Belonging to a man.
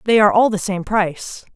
No: female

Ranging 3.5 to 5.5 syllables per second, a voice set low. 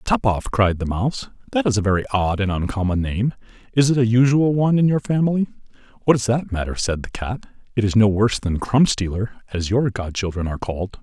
No: 6.0 syllables/s; low, 115 Hz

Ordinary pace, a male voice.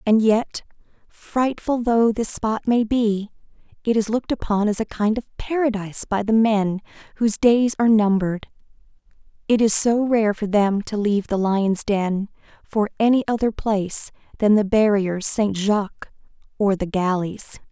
No: average, 160 wpm; female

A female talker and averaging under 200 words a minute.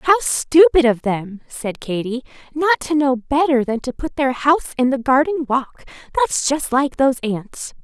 Yes: female; average, 185 wpm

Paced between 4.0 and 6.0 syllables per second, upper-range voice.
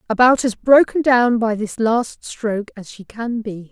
Yes: 4.3 syllables/s; high, 230 Hz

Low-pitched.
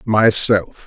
Yes: low, 105 Hz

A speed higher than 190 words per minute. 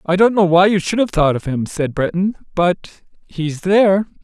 Yes: average, 200 wpm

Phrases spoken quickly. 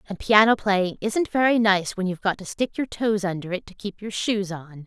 Yes: fast, 245 wpm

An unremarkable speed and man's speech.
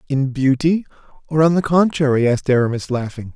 Yes: average, 160 wpm; male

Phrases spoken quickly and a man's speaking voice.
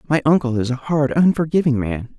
No: average, 190 wpm; male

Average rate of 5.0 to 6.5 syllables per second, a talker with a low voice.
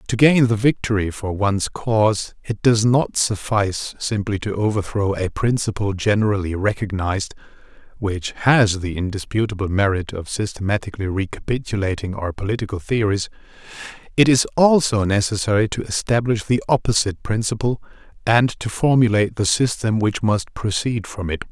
Yes: 5.2 syllables/s; low, 105 Hz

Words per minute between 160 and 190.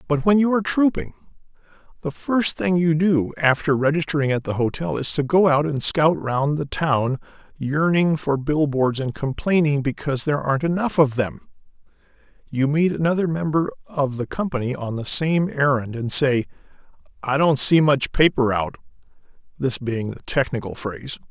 Yes: average, 165 wpm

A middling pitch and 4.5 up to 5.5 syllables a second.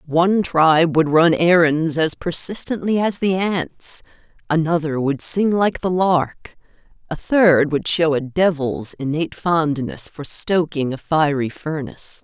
No: medium, 165 Hz; 4.1 syllables/s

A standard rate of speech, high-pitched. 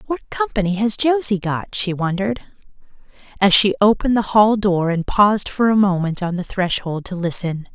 Yes: average, 180 wpm; high, 200 Hz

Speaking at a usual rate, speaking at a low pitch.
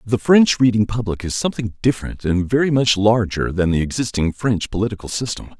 Yes: average, 180 wpm; low, 110 Hz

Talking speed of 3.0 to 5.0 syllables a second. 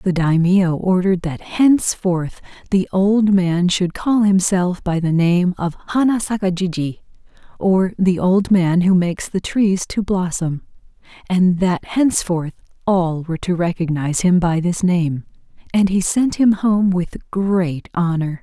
Yes: 4.2 syllables/s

